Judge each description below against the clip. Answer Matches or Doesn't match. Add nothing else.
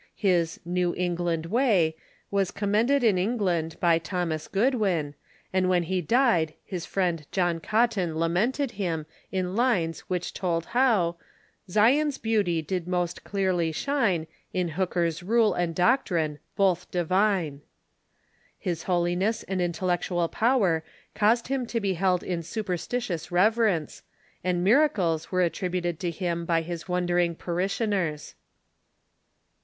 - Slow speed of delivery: Matches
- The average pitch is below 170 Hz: Doesn't match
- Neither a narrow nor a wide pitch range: Matches